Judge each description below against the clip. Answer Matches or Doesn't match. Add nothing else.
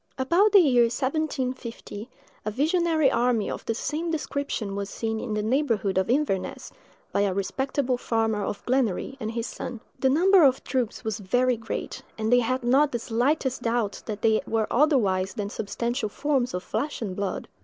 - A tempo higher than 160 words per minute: Matches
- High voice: Matches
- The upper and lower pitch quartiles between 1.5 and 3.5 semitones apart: Doesn't match